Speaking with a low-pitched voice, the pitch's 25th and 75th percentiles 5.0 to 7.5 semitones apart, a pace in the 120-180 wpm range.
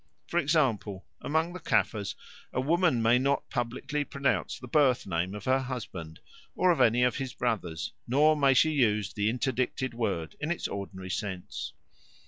Yes: low, 125 Hz; wide, 5.6 semitones; average, 165 wpm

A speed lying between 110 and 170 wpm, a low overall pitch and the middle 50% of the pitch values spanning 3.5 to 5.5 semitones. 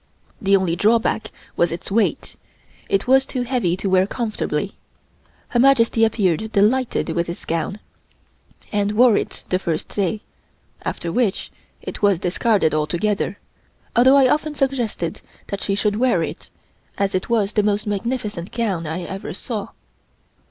No: average, 150 wpm; high, 205 Hz; average, 4.1 semitones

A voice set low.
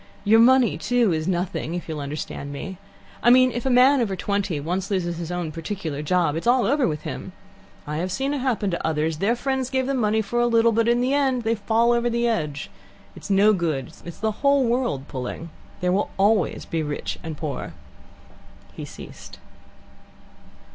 No: high, 200 Hz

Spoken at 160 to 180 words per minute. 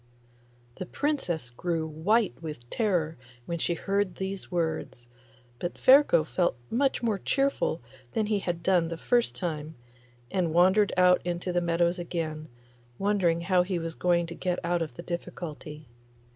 No: average, 150 wpm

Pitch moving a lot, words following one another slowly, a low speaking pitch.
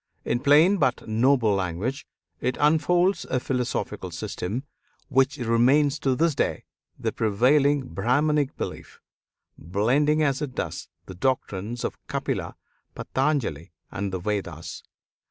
Yes: wide, 5.7 semitones; slow, 120 wpm; low, 130 Hz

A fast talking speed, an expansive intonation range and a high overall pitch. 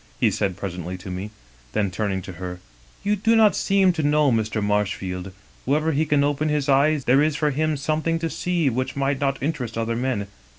No: fast, 210 wpm; wide, 7.1 semitones; low, 135 Hz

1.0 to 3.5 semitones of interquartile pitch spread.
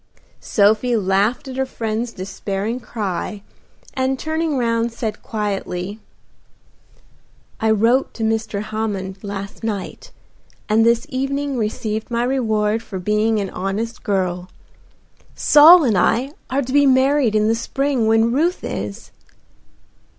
No: average, 3.9 semitones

